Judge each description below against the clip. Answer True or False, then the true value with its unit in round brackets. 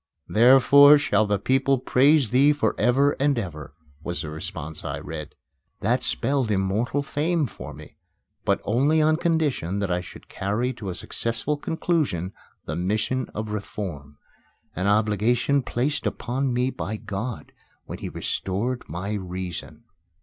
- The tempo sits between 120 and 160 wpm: True (145 wpm)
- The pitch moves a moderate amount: False (6.5 semitones)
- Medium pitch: False (110 Hz)